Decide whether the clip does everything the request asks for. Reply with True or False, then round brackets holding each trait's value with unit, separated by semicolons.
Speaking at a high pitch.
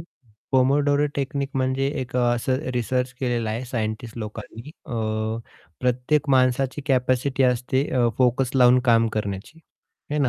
False (130 Hz)